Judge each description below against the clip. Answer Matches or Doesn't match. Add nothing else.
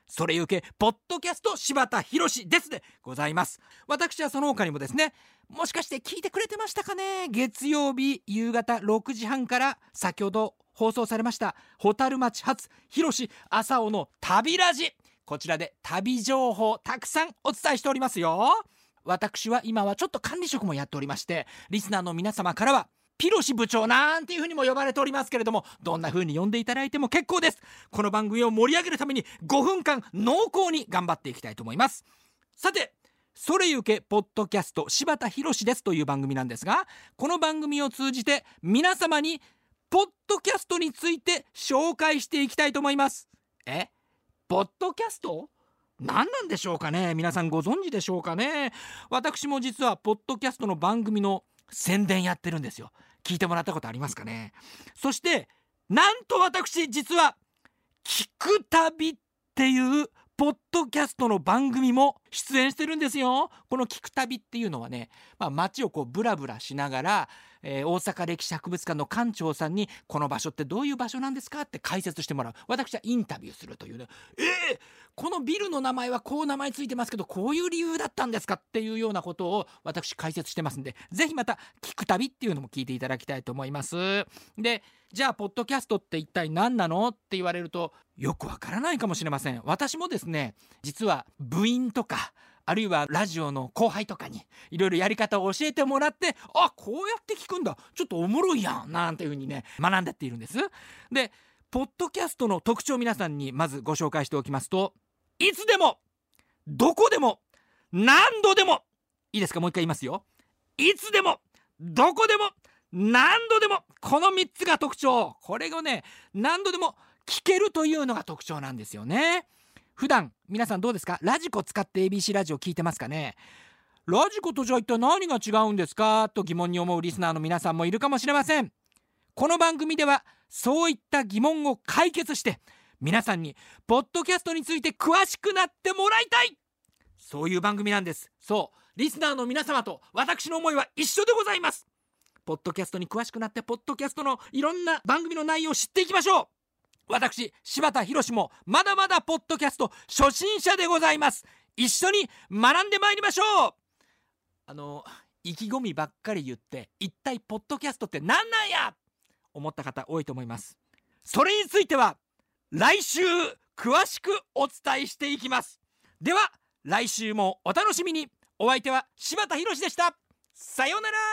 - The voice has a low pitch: Doesn't match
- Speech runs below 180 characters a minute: Doesn't match